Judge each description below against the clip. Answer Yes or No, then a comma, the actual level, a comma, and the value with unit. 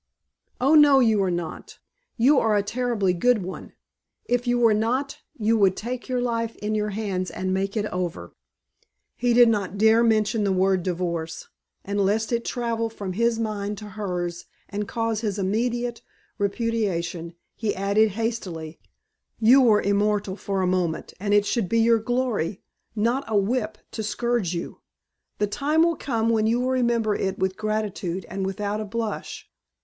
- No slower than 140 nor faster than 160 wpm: No, average, 170 wpm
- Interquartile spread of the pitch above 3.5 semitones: No, average, 3.2 semitones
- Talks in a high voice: Yes, high, 215 Hz